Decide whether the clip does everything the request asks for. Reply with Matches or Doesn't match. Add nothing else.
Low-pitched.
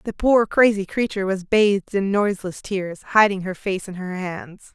Doesn't match